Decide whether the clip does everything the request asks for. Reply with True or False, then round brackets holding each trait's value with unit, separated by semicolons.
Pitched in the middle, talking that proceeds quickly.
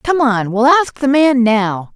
False (250 Hz; 215 wpm)